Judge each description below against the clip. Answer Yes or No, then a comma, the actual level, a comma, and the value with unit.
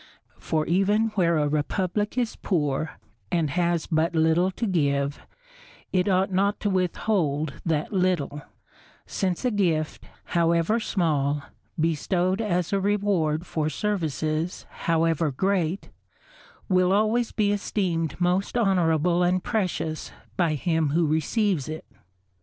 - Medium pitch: Yes, medium, 175 Hz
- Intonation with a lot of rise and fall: No, average, 3.7 semitones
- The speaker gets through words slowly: Yes, slow, 125 wpm